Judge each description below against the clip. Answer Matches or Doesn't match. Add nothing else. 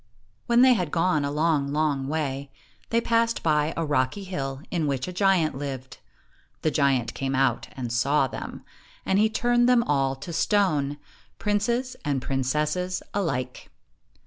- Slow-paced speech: Doesn't match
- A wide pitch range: Matches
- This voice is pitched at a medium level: Matches